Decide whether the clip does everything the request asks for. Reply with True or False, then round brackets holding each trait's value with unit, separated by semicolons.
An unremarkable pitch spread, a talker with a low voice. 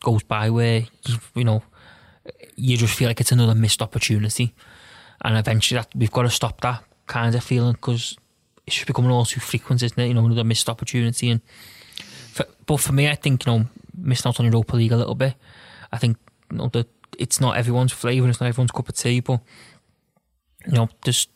False (1.5 semitones; 120 Hz)